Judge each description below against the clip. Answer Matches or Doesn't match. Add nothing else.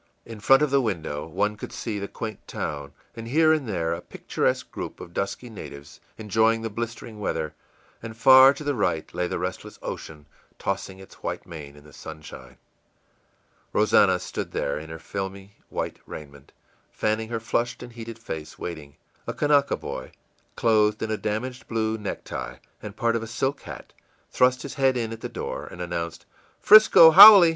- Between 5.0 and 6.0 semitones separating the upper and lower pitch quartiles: Matches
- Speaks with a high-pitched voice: Doesn't match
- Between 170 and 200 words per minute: Matches